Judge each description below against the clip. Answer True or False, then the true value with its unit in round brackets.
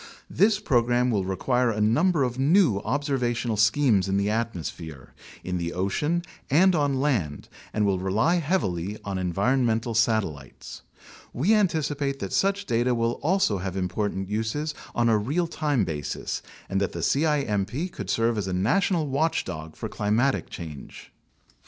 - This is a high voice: False (115 Hz)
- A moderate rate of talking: True (155 wpm)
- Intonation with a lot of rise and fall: True (6.9 semitones)